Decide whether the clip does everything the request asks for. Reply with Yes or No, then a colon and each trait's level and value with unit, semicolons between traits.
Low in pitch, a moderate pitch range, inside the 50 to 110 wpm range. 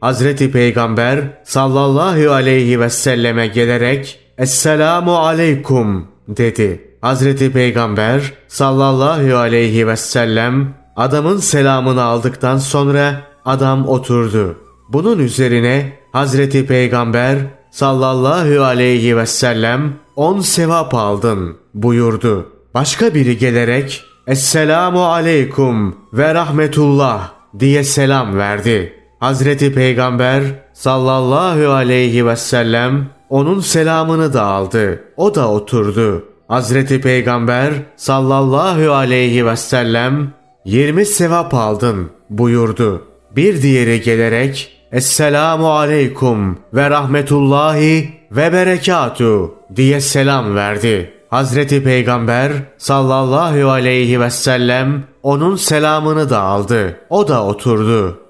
Yes: low, 130 Hz; average, 3.2 semitones; slow, 95 wpm